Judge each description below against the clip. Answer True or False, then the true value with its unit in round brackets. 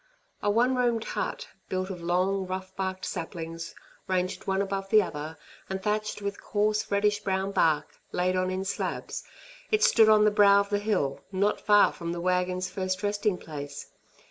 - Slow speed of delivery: False (175 wpm)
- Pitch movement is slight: True (2.2 semitones)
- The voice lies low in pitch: False (190 Hz)